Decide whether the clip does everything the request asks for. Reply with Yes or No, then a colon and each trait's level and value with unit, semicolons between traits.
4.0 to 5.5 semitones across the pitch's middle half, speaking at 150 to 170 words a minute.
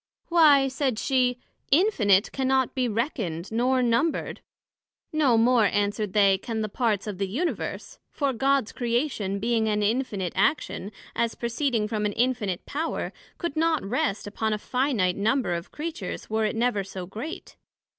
Yes: average, 4.5 semitones; average, 155 wpm